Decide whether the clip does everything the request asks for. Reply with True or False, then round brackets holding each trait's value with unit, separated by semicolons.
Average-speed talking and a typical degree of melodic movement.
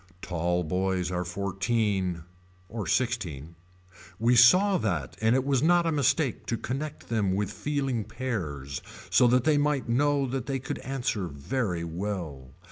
False (150 wpm; 6.9 semitones)